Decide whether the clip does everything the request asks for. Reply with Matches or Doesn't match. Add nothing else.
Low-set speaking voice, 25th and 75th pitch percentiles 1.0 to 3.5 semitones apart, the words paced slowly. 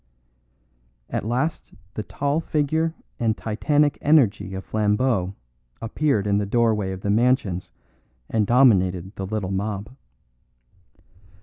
Doesn't match